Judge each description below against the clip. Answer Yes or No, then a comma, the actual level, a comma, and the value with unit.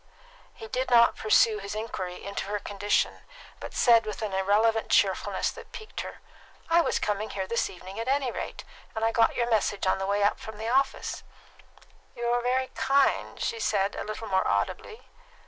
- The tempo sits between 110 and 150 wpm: No, average, 190 wpm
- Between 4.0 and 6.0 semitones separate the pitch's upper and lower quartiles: No, average, 2.9 semitones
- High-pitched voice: Yes, high, 220 Hz